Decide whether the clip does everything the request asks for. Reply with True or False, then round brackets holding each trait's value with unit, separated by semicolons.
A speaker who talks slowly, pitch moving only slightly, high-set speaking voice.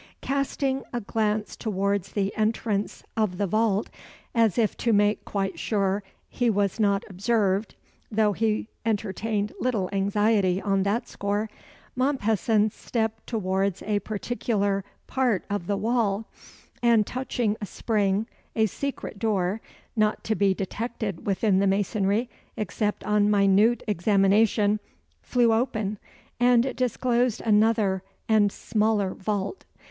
True (125 wpm; 2.2 semitones; 210 Hz)